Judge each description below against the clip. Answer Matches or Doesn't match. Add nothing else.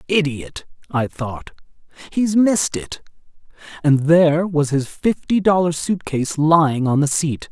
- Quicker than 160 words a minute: Doesn't match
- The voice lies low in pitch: Doesn't match